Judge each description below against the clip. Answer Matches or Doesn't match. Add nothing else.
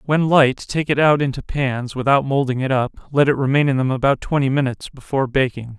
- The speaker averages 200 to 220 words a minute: Matches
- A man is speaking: Matches